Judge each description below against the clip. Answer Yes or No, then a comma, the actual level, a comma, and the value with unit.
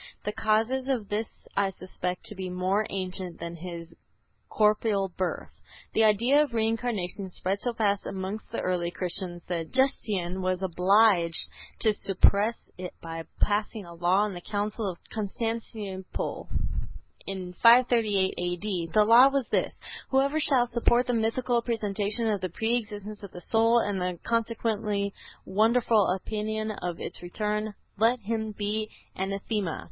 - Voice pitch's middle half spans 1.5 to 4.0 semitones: Yes, average, 3.3 semitones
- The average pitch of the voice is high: Yes, high, 210 Hz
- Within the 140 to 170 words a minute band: Yes, average, 145 wpm